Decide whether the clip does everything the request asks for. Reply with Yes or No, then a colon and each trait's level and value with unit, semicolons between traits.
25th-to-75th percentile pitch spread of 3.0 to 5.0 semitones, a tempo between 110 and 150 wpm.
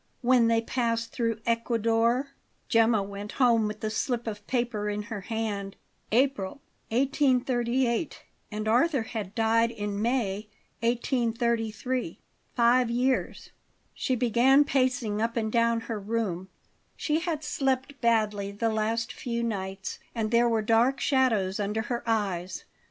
No: narrow, 2.4 semitones; slow, 135 wpm